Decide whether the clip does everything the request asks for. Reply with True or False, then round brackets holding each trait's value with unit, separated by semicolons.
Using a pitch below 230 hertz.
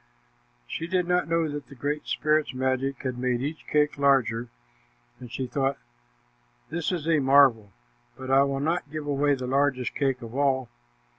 True (140 Hz)